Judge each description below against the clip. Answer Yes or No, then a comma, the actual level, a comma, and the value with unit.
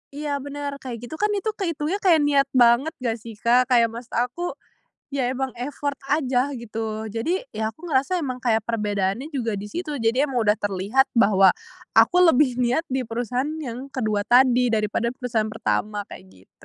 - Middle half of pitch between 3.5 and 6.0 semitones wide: Yes, average, 4.0 semitones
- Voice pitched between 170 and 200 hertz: No, very high, 250 Hz